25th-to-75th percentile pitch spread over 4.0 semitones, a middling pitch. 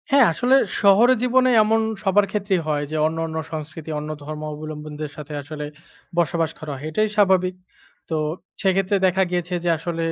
Yes: average, 4.5 semitones; medium, 170 Hz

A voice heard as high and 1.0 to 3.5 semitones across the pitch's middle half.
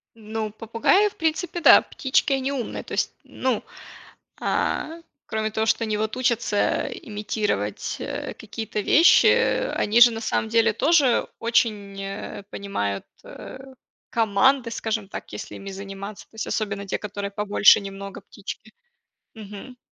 Yes: high, 220 Hz; average, 3.0 semitones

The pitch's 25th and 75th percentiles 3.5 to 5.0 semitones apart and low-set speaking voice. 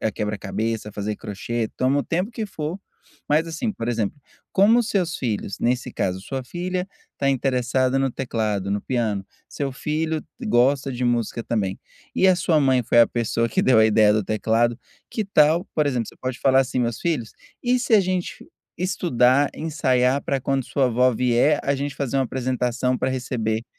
Yes: average, 4.6 semitones; low, 130 Hz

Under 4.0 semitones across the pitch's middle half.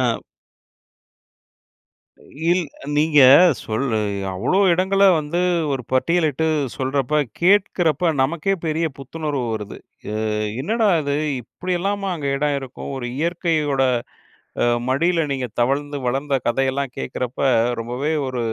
No: average, 4.3 semitones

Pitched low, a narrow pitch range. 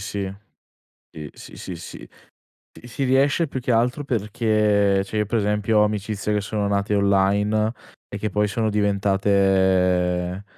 Yes: low, 105 Hz; narrow, 1.8 semitones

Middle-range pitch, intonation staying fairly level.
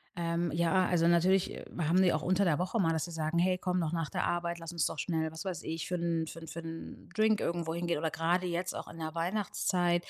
Yes: medium, 170 Hz; narrow, 1.7 semitones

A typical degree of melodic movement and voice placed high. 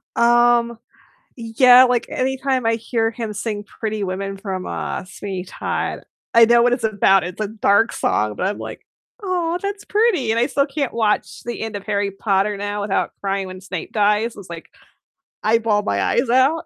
Yes: average, 3.4 semitones; high, 225 Hz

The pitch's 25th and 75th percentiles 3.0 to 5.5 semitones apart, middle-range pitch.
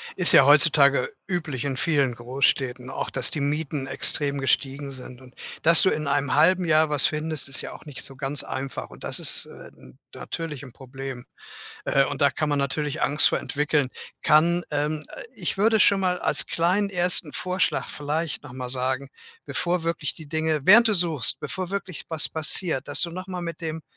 Yes: average, 3.7 semitones; medium, 150 Hz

